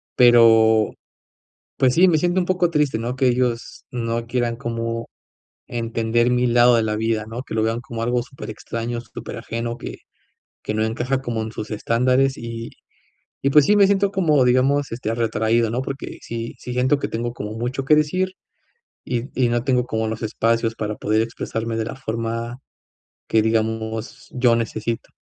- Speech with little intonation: Yes, narrow, 2.1 semitones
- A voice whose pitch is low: Yes, low, 120 Hz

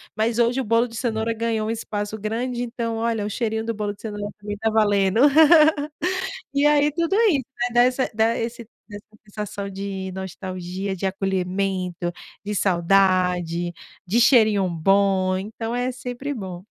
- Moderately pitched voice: No, high, 210 Hz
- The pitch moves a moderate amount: Yes, average, 3.3 semitones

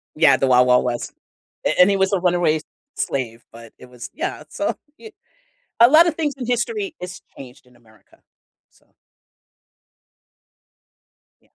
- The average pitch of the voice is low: No, medium, 175 Hz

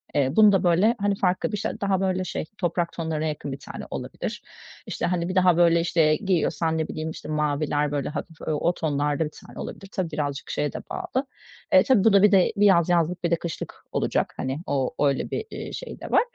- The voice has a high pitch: No, medium, 170 Hz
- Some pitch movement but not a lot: Yes, average, 3.8 semitones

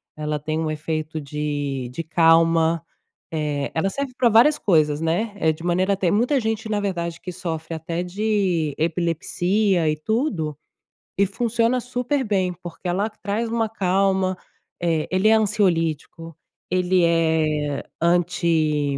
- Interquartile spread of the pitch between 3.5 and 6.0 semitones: Yes, average, 4.3 semitones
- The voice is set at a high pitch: No, medium, 170 Hz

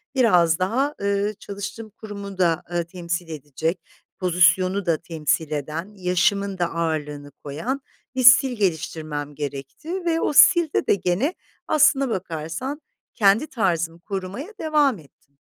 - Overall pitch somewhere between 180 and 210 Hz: Yes, medium, 185 Hz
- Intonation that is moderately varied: No, wide, 5.7 semitones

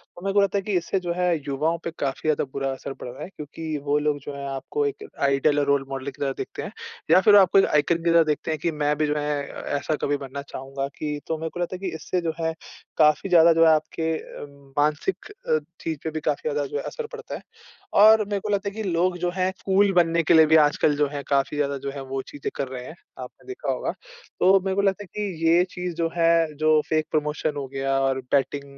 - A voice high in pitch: No, medium, 160 Hz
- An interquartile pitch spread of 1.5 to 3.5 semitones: No, average, 4.0 semitones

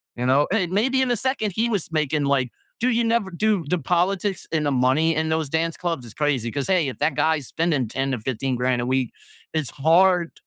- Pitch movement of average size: No, wide, 6.0 semitones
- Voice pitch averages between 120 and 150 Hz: No, medium, 160 Hz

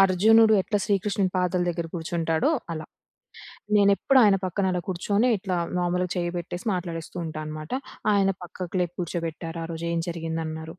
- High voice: No, medium, 175 Hz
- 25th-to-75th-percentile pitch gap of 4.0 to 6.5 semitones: No, average, 2.8 semitones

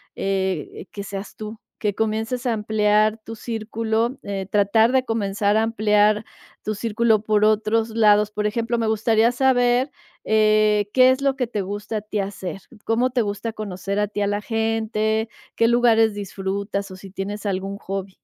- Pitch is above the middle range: Yes, high, 215 Hz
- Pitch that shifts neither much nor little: No, narrow, 1.8 semitones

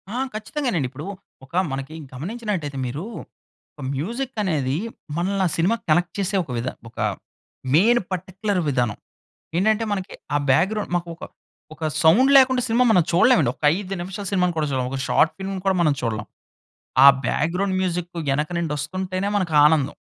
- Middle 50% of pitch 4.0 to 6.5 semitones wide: Yes, average, 5.2 semitones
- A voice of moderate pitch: Yes, medium, 180 Hz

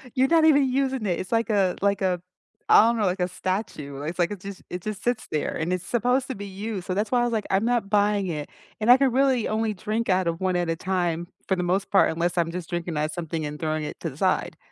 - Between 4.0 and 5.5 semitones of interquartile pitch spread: Yes, average, 4.5 semitones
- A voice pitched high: Yes, high, 195 Hz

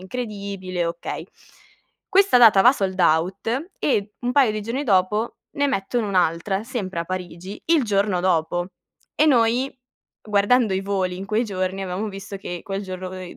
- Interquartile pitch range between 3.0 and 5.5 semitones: Yes, average, 3.7 semitones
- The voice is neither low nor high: No, high, 200 Hz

